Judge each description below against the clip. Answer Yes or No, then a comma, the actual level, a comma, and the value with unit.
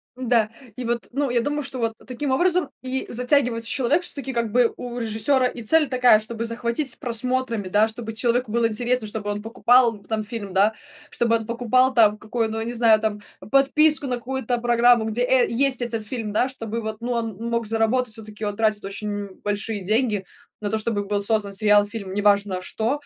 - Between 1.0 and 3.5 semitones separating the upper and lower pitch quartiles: Yes, narrow, 2.6 semitones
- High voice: Yes, high, 230 Hz